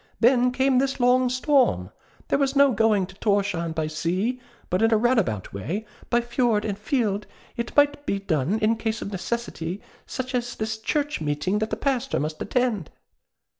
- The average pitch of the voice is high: Yes, high, 220 Hz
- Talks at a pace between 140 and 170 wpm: No, average, 180 wpm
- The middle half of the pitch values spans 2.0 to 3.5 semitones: No, average, 4.6 semitones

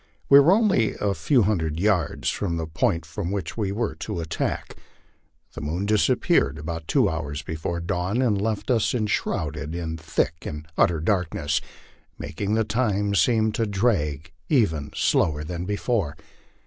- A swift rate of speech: No, average, 160 wpm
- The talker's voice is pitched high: No, very low, 90 Hz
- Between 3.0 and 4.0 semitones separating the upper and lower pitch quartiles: No, average, 5.1 semitones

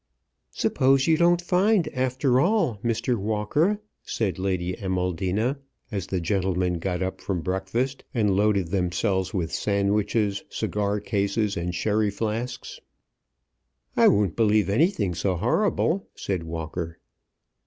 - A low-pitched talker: Yes, low, 100 Hz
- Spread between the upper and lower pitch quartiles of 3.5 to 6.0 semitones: Yes, average, 4.7 semitones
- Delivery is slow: Yes, slow, 120 wpm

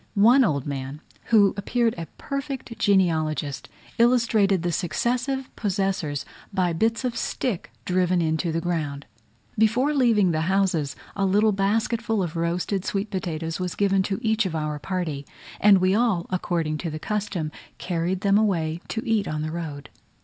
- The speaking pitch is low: No, high, 190 Hz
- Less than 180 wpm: Yes, average, 155 wpm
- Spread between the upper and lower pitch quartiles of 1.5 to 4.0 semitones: No, average, 4.9 semitones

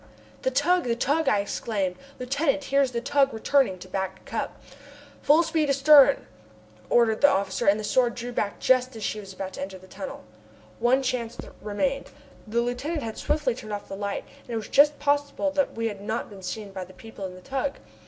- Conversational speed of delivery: No, fast, 210 wpm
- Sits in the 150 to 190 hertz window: No, high, 240 Hz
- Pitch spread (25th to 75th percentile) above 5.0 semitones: Yes, wide, 5.5 semitones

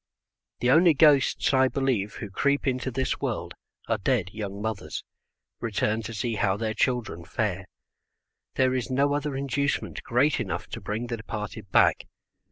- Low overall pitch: Yes, low, 120 Hz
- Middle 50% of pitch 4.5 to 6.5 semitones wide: No, average, 4.0 semitones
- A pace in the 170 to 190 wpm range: No, average, 160 wpm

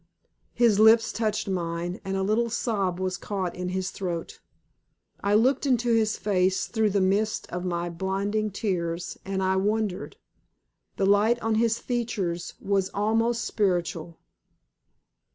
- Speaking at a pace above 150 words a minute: No, average, 140 wpm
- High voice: Yes, high, 200 Hz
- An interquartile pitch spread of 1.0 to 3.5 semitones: Yes, average, 3.1 semitones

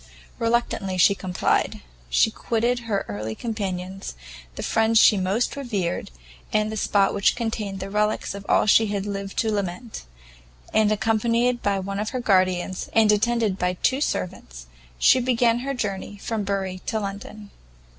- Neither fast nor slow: Yes, average, 160 wpm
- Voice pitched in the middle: No, high, 205 Hz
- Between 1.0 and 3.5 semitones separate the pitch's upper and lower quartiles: Yes, average, 2.9 semitones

